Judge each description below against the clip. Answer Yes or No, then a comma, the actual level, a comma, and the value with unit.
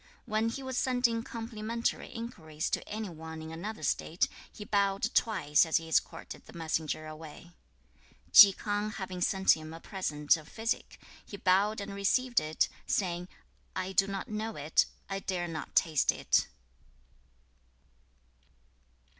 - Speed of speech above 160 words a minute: No, average, 145 wpm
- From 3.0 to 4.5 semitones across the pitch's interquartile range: No, average, 5.1 semitones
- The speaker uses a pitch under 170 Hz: No, high, 195 Hz